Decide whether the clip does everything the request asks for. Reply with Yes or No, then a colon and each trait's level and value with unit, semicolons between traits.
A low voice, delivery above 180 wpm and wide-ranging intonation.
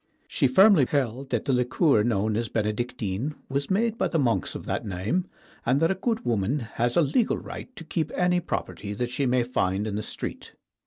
Yes: low, 125 Hz; fast, 205 wpm; wide, 6.8 semitones